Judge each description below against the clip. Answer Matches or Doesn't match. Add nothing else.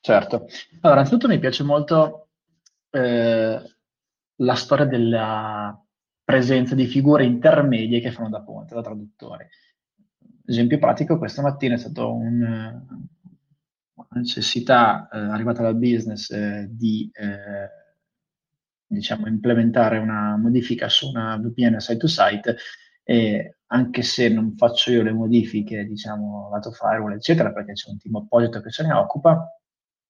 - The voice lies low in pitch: Matches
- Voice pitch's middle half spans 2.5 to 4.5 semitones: Doesn't match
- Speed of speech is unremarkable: Matches